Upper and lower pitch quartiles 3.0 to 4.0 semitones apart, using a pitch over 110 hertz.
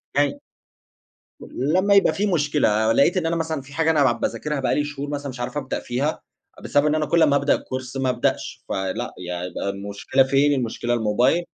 Yes: average, 3.7 semitones; medium, 140 Hz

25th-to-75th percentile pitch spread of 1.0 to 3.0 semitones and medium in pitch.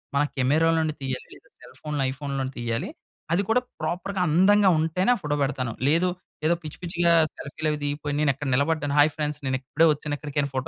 Yes: average, 2.7 semitones; medium, 150 Hz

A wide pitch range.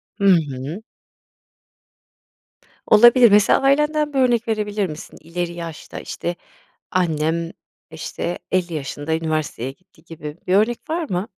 Yes: wide, 5.8 semitones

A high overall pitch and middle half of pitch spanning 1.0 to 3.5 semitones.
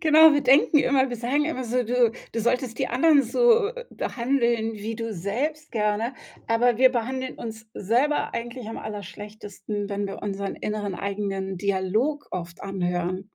No: high, 230 Hz; average, 4.3 semitones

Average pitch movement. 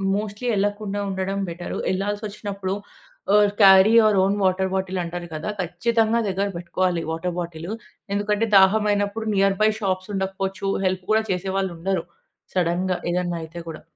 No: narrow, 2.1 semitones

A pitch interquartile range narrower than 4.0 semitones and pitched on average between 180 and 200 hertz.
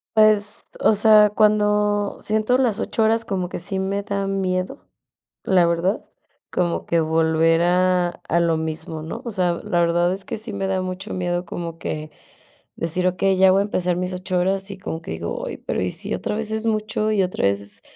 Yes: average, 3.2 semitones; high, 190 Hz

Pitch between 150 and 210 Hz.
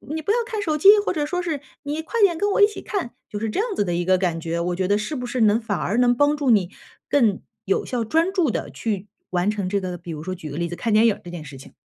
No: high, 220 Hz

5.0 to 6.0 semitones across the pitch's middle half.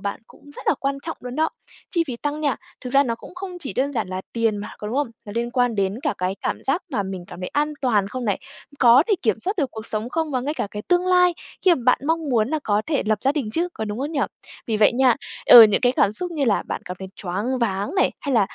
Yes: wide, 5.6 semitones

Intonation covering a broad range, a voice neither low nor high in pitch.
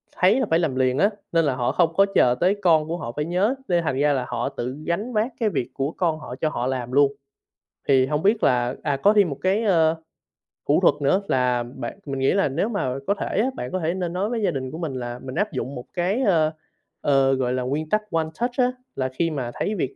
Yes: wide, 6.3 semitones; medium, 155 Hz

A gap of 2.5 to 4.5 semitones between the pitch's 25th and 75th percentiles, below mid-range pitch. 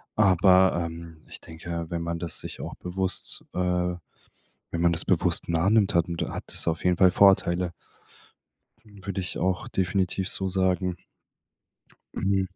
No: narrow, 1.9 semitones; very low, 90 Hz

